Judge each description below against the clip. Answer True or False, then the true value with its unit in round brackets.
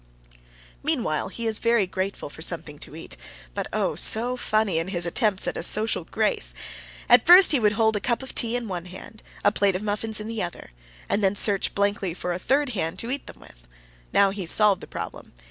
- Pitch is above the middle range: True (205 Hz)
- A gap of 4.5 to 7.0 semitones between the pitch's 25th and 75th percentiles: False (3.9 semitones)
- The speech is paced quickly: True (215 wpm)